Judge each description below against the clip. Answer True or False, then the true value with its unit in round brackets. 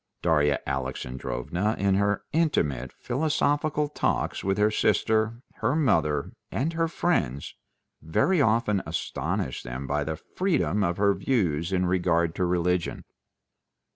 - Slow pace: True (125 wpm)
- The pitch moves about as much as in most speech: False (8.1 semitones)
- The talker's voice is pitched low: True (95 Hz)